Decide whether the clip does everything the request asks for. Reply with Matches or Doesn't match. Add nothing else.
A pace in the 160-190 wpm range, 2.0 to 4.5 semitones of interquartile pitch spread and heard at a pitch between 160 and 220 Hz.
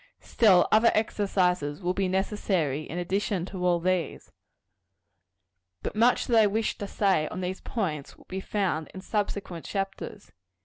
Doesn't match